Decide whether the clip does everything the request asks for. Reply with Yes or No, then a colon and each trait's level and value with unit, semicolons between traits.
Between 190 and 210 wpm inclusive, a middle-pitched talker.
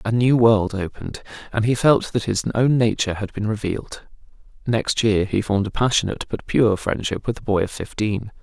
No: average, 200 wpm; low, 110 Hz